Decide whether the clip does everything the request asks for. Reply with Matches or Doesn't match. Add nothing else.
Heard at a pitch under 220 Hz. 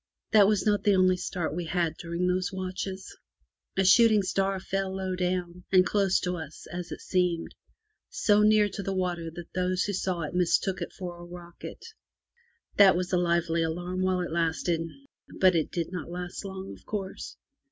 Matches